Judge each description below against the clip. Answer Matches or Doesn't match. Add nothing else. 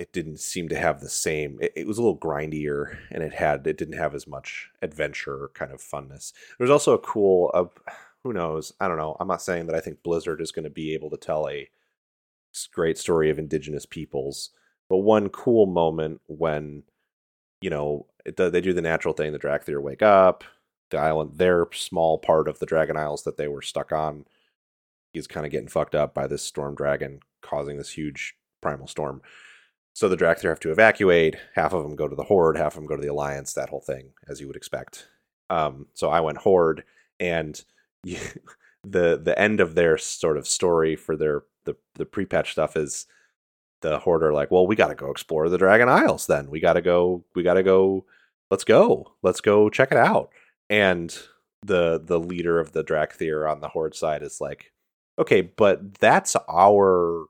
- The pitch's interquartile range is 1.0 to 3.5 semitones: Matches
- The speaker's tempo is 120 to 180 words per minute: Doesn't match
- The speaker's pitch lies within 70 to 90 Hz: Matches